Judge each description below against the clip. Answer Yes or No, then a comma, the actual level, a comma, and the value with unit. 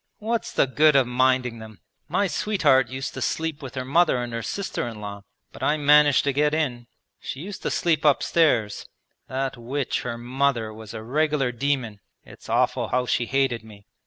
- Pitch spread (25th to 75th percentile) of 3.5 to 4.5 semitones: Yes, average, 4.0 semitones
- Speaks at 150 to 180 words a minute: No, average, 190 wpm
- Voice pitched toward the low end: Yes, low, 130 Hz